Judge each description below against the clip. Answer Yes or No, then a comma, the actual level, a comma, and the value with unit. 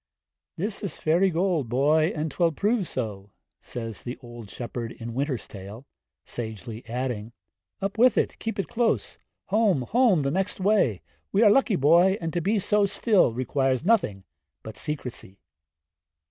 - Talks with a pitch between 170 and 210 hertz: No, medium, 150 Hz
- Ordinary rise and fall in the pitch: No, wide, 8.6 semitones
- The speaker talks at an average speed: Yes, average, 160 wpm